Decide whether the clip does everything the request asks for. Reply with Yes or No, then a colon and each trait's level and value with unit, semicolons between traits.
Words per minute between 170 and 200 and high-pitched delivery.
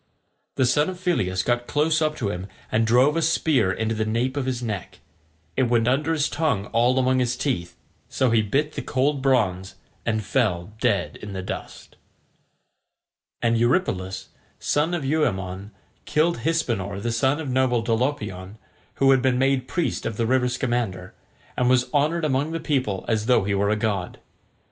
No: average, 175 wpm; low, 125 Hz